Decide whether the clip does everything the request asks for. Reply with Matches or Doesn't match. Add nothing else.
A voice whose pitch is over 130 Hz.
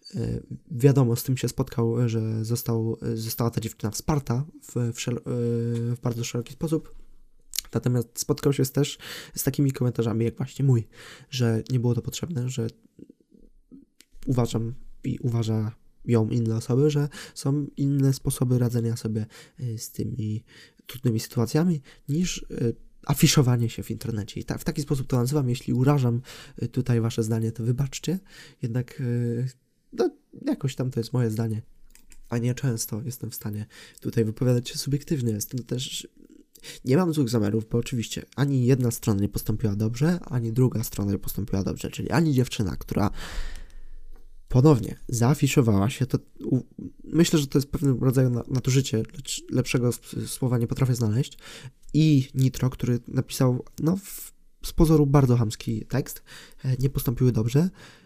Doesn't match